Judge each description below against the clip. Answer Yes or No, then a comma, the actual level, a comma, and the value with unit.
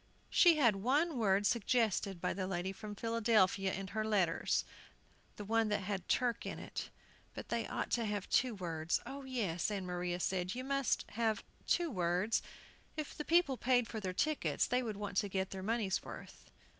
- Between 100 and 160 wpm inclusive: No, average, 185 wpm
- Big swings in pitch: No, average, 4.1 semitones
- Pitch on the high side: Yes, high, 210 Hz